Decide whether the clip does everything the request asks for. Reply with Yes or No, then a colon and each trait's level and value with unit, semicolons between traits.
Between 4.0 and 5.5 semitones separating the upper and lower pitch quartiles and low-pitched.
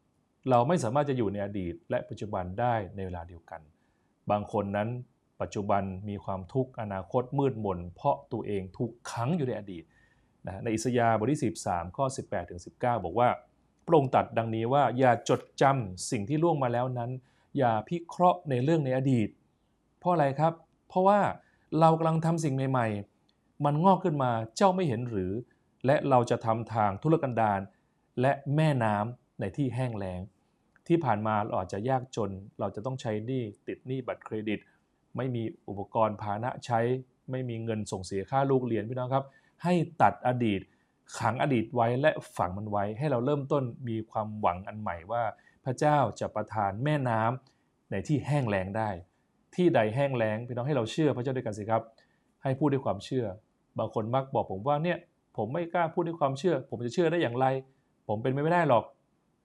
Yes: average, 4.7 semitones; low, 120 Hz